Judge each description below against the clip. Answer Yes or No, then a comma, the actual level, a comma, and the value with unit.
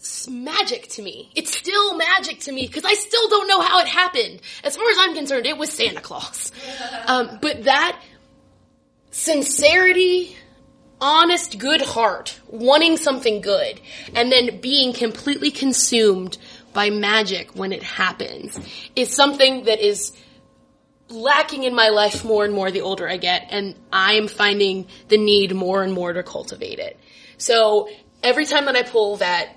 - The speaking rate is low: No, average, 160 wpm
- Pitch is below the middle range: No, very high, 260 Hz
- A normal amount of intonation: No, wide, 6.6 semitones